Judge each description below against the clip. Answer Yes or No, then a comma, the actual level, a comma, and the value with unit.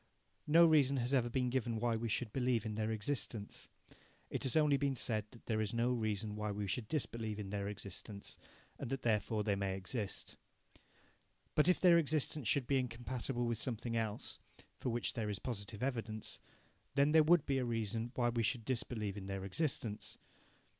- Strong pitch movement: No, average, 3.6 semitones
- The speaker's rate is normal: Yes, average, 190 wpm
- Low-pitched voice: Yes, low, 115 Hz